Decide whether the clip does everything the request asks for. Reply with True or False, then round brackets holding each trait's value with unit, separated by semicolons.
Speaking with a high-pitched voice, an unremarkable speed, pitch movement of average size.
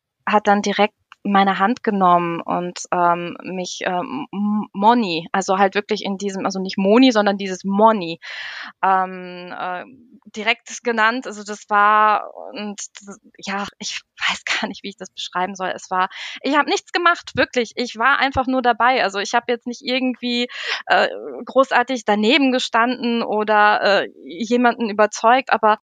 True (210 Hz; 155 wpm; 3.8 semitones)